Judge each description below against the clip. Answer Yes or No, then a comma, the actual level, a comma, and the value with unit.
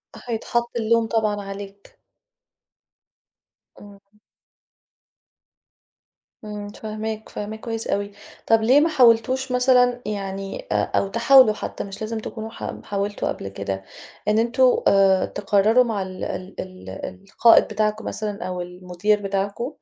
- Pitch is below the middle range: No, high, 215 Hz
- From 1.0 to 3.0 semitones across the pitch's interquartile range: Yes, average, 2.7 semitones